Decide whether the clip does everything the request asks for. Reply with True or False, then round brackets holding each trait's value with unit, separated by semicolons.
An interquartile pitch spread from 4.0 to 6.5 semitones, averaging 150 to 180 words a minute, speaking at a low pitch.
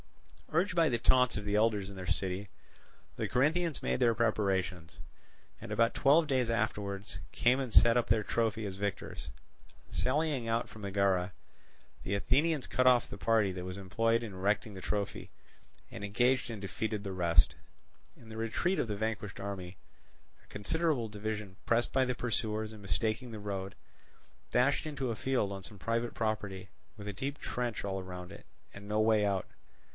False (3.5 semitones; 175 wpm; 110 Hz)